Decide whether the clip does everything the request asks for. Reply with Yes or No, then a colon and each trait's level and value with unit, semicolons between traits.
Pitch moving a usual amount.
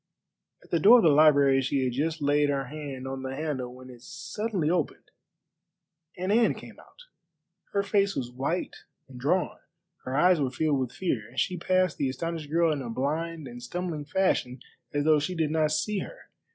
Yes: average, 4.5 semitones